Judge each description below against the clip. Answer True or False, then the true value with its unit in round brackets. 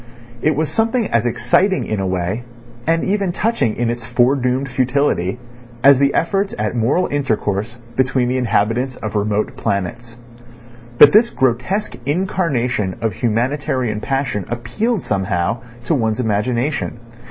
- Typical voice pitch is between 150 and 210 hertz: False (125 Hz)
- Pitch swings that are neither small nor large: True (4.7 semitones)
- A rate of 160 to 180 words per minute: False (135 wpm)